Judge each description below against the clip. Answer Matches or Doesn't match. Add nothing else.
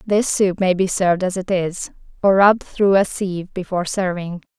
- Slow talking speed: Doesn't match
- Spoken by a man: Doesn't match